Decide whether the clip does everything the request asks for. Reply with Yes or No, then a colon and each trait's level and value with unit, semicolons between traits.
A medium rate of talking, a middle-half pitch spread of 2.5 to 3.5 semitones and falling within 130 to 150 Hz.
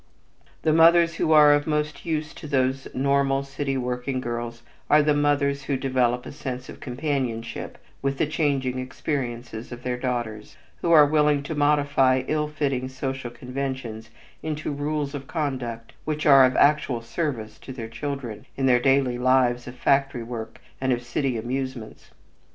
Yes: average, 160 wpm; average, 2.9 semitones; low, 135 Hz